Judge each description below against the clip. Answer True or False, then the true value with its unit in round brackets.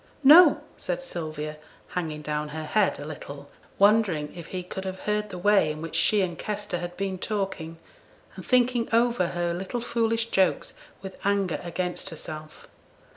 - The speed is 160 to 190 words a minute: True (165 wpm)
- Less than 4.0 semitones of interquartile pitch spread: False (4.7 semitones)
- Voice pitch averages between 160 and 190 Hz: True (185 Hz)